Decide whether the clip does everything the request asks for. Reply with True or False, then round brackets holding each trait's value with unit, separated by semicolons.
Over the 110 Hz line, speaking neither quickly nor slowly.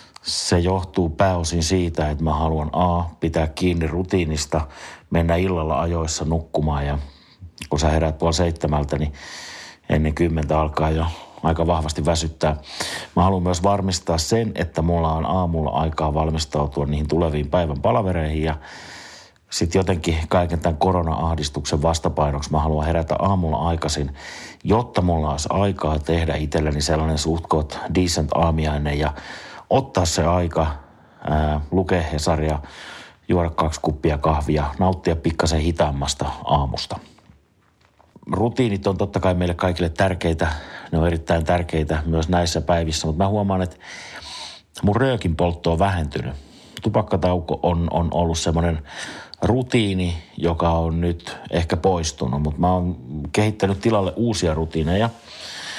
False (85 Hz; 130 wpm)